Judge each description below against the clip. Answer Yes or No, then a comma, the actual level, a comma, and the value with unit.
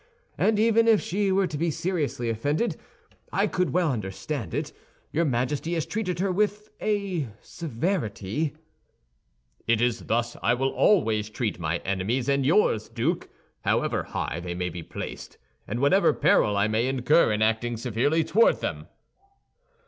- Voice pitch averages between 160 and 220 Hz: No, low, 135 Hz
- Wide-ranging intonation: Yes, wide, 8.4 semitones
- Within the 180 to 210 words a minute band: No, average, 155 wpm